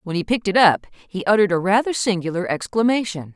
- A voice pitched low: No, high, 200 Hz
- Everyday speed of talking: Yes, average, 195 wpm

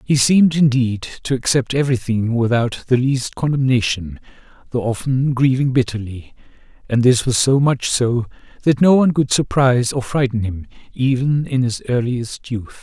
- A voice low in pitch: Yes, low, 125 Hz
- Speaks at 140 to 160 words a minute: Yes, average, 155 wpm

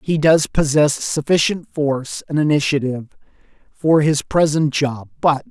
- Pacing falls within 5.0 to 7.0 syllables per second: No, 4.6 syllables/s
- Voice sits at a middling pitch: Yes, medium, 145 Hz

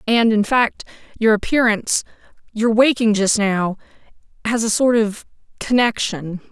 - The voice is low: No, high, 220 Hz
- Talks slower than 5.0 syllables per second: Yes, 4.5 syllables/s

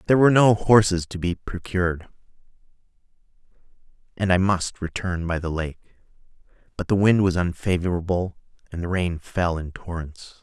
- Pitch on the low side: Yes, very low, 90 Hz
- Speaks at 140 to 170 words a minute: Yes, average, 145 wpm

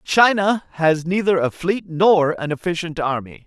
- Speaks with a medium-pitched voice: Yes, medium, 170 Hz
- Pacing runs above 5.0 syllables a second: No, 4.4 syllables/s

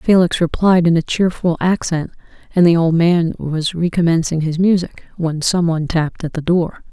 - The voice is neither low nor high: Yes, medium, 170 Hz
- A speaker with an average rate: Yes, average, 175 wpm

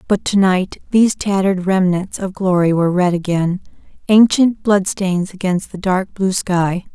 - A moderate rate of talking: Yes, average, 155 wpm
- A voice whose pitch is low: No, high, 190 Hz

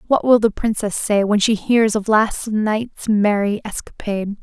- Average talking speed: Yes, average, 175 wpm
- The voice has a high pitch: Yes, high, 215 Hz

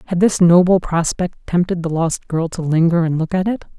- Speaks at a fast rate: Yes, fast, 220 wpm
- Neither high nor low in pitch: Yes, medium, 170 Hz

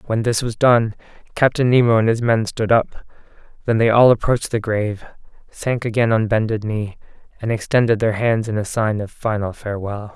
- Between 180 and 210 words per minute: Yes, average, 190 wpm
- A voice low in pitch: Yes, low, 110 Hz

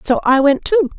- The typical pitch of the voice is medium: No, very high, 305 Hz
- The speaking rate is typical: No, fast, 245 wpm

